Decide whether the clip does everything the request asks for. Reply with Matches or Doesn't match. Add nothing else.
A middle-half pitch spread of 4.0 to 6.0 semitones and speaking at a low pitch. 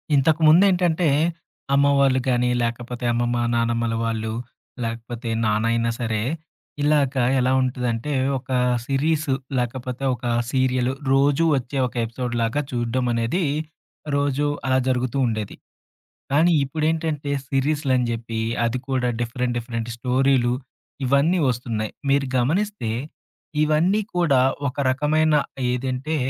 Doesn't match